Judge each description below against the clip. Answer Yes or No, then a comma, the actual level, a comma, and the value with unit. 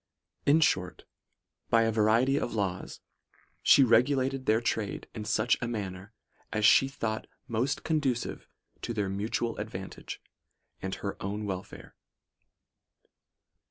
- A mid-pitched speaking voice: No, low, 110 Hz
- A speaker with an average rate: No, slow, 125 wpm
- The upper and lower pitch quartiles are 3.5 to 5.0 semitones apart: Yes, average, 3.8 semitones